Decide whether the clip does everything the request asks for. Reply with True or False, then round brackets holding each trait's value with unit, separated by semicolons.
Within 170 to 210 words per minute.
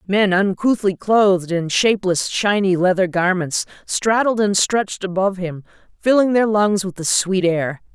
False (150 wpm)